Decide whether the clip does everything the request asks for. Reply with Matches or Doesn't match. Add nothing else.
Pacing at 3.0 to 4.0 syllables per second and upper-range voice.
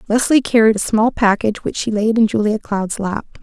Doesn't match